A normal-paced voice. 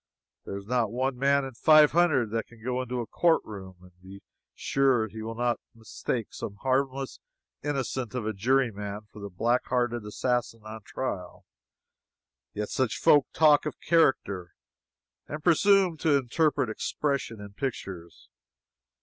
Yes: average, 155 wpm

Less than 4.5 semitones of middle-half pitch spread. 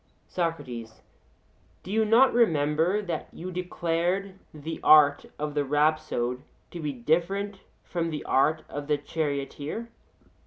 Yes: average, 3.9 semitones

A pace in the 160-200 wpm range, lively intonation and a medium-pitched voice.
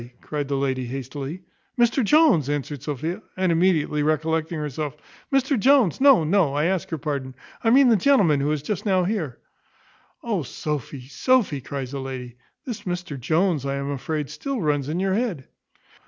Yes: average, 170 wpm; wide, 5.8 semitones; medium, 155 Hz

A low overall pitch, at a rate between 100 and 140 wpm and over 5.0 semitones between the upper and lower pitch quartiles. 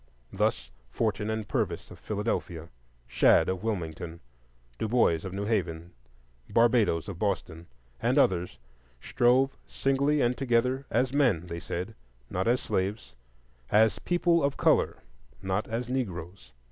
Yes: low, 105 Hz; slow, 135 wpm; wide, 5.6 semitones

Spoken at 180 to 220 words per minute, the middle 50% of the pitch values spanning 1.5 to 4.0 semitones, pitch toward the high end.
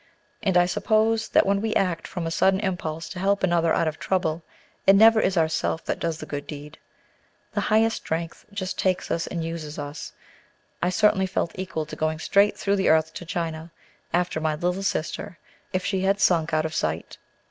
No: average, 200 wpm; average, 3.4 semitones; medium, 175 Hz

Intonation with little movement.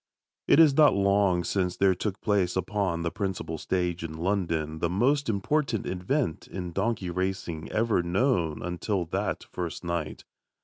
No: average, 3.1 semitones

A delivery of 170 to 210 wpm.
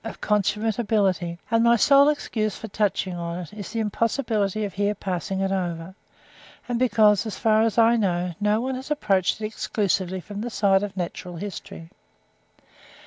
Yes: average, 175 wpm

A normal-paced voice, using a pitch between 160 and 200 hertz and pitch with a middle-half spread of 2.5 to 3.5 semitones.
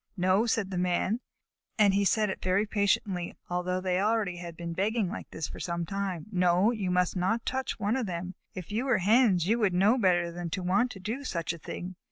No: fast, 225 wpm; high, 190 Hz; average, 3.2 semitones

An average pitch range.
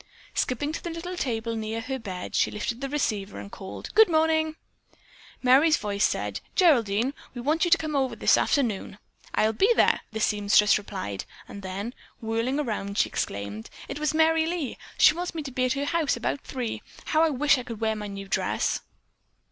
No: wide, 6.7 semitones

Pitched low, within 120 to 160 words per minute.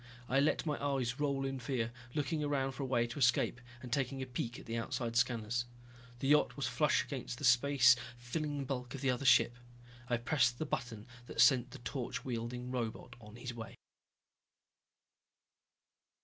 No: low, 125 Hz; average, 175 wpm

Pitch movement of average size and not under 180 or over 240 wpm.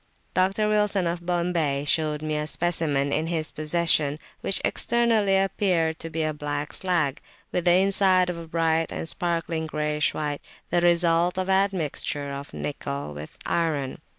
No: average, 3.0 semitones; average, 165 wpm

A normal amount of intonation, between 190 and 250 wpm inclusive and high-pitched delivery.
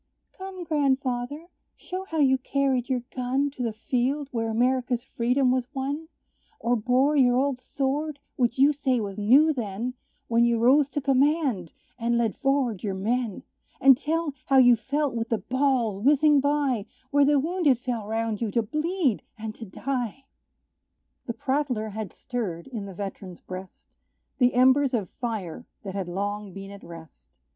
No: average, 4.0 semitones; average, 165 wpm; very high, 250 Hz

